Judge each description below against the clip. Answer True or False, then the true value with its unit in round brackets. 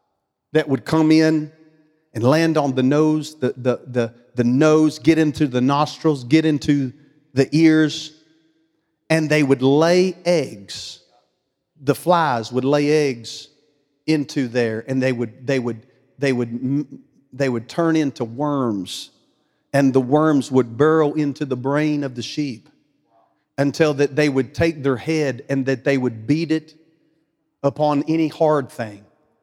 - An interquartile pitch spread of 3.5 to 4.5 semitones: False (3.1 semitones)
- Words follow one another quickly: False (155 wpm)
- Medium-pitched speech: True (145 Hz)